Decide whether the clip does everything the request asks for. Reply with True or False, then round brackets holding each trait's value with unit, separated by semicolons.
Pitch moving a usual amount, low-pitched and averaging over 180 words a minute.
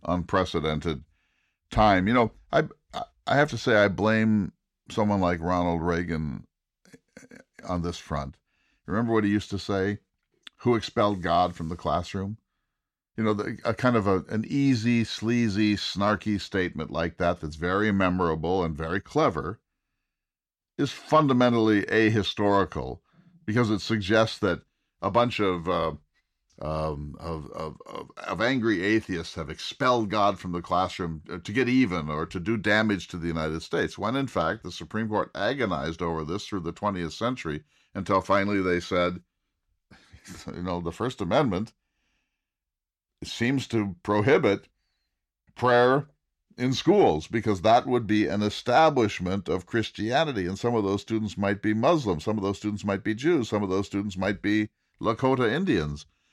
False (4.1 semitones; 100 Hz; 155 wpm)